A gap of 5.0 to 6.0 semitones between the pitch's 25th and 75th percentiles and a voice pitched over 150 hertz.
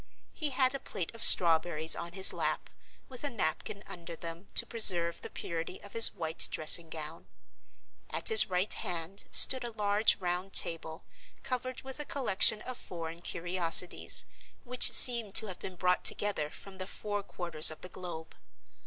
No: average, 4.6 semitones; medium, 185 Hz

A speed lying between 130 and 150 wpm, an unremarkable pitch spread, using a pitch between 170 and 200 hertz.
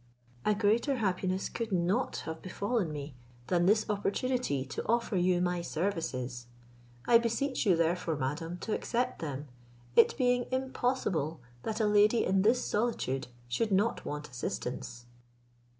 No: average, 140 wpm; wide, 6.2 semitones; high, 190 Hz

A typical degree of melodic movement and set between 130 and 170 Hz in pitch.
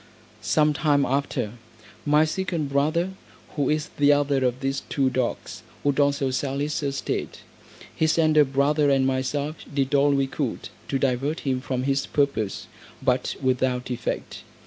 No: narrow, 2.0 semitones; medium, 140 Hz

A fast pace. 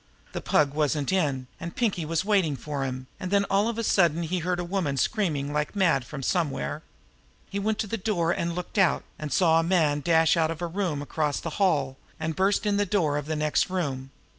Yes: fast, 225 wpm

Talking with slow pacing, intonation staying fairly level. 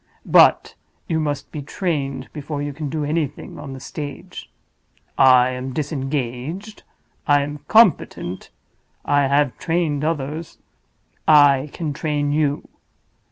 Yes: slow, 110 wpm; narrow, 2.3 semitones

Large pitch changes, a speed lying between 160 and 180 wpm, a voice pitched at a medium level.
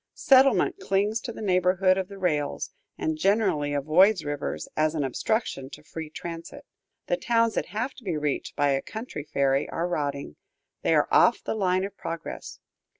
Yes: wide, 5.7 semitones; average, 175 wpm; medium, 175 Hz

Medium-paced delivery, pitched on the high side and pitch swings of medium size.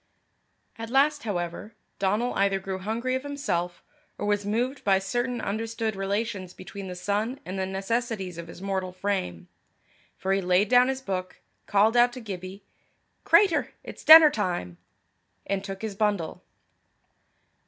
Yes: average, 150 wpm; high, 200 Hz; average, 3.9 semitones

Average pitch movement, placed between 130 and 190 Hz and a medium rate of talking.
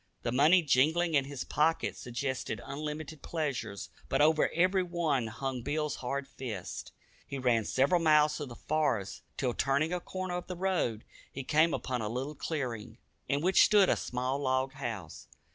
Yes: average, 3.9 semitones; medium, 140 Hz; average, 170 wpm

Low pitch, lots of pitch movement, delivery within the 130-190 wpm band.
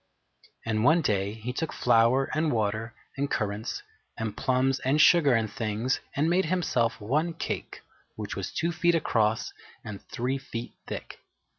Yes: low, 125 Hz; wide, 5.7 semitones; average, 155 wpm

